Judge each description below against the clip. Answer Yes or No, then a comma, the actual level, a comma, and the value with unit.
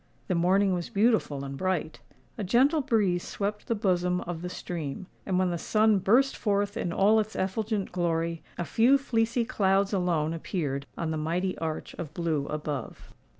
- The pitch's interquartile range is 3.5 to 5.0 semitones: Yes, average, 4.2 semitones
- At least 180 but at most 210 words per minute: No, average, 170 wpm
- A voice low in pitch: No, medium, 185 Hz